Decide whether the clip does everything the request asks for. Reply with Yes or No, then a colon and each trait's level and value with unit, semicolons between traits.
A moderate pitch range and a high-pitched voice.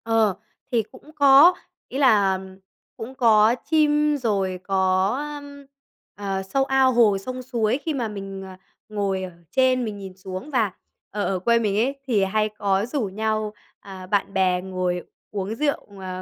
Yes: average, 4.8 semitones; high, 210 Hz